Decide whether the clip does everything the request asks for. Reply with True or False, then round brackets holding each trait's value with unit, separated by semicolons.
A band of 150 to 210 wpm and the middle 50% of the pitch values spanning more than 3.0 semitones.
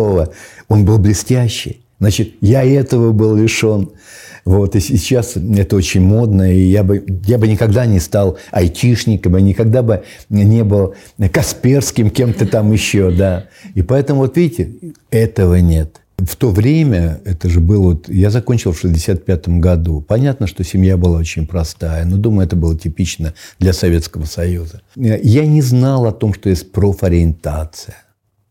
True (155 wpm; 3.8 semitones)